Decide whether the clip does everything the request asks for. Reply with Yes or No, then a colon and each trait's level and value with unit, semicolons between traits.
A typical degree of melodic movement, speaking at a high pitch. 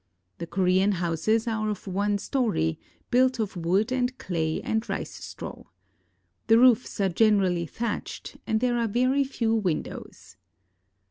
Yes: average, 4.6 semitones; high, 215 Hz